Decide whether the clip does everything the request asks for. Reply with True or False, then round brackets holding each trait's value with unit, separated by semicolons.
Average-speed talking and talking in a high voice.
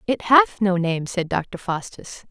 True (180 wpm; 200 Hz)